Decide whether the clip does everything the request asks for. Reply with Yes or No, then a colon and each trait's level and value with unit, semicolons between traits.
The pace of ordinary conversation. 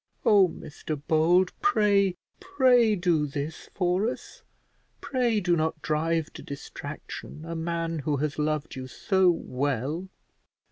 No: slow, 130 wpm